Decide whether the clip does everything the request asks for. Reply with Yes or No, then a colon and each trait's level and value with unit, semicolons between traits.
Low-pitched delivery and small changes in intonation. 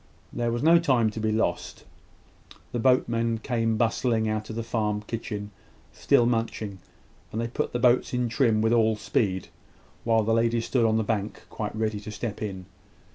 Yes: low, 115 Hz; narrow, 1.6 semitones